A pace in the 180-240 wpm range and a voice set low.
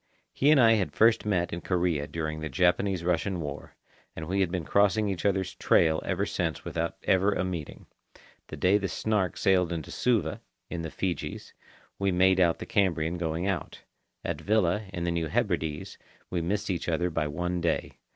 Yes: average, 190 wpm; very low, 90 Hz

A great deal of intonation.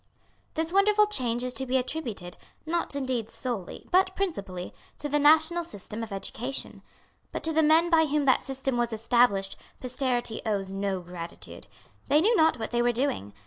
Yes: wide, 6.3 semitones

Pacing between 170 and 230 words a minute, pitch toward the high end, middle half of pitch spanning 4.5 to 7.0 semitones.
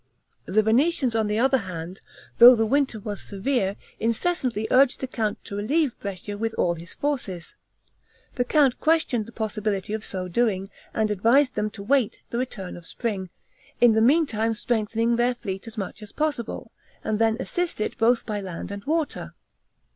No: average, 175 wpm; high, 225 Hz; average, 3.7 semitones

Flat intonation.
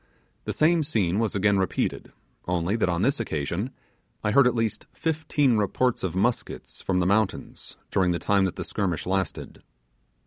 No: average, 4.7 semitones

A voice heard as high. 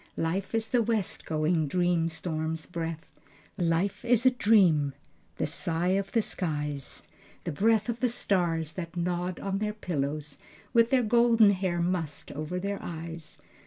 No: medium, 180 Hz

